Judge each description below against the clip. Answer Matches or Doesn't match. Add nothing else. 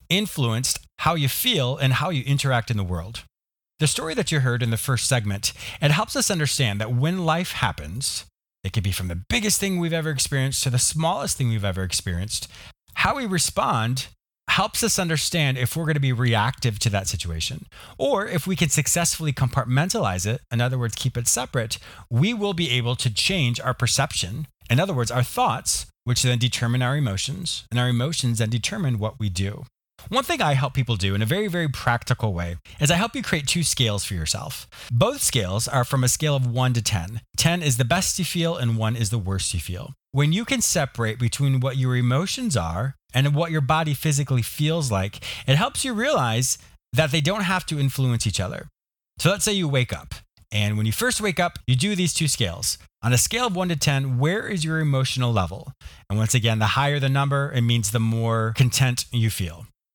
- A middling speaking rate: Doesn't match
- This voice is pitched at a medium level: Doesn't match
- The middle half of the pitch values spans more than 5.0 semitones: Matches